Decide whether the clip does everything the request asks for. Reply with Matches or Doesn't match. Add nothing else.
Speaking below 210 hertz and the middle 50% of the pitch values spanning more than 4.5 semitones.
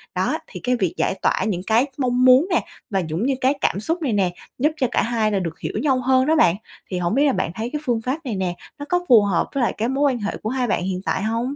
Doesn't match